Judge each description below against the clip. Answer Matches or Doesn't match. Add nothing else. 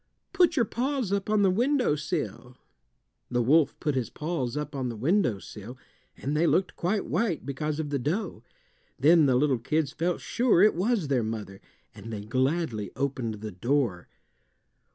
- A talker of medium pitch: Matches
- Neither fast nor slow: Matches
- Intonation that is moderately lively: Doesn't match